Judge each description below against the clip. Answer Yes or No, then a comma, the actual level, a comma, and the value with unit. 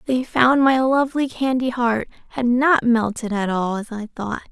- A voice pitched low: No, high, 240 Hz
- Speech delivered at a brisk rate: No, average, 185 wpm